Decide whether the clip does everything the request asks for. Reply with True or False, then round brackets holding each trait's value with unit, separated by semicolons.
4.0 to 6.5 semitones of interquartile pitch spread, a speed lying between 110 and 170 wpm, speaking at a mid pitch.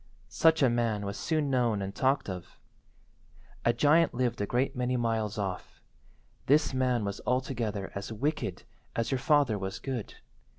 False (4.5 semitones; 160 wpm; 120 Hz)